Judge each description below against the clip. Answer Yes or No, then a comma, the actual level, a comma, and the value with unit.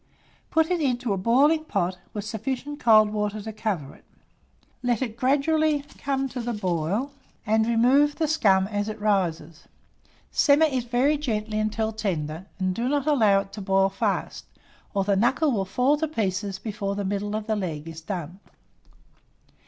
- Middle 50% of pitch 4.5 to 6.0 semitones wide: Yes, average, 5.2 semitones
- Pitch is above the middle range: Yes, high, 215 Hz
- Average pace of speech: Yes, average, 170 wpm